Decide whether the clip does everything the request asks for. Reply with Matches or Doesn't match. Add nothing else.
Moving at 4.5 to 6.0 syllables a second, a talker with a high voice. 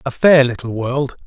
Doesn't match